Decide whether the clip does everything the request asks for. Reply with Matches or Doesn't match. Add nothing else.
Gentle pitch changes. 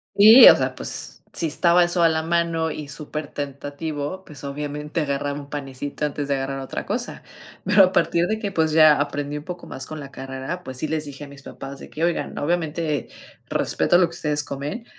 Doesn't match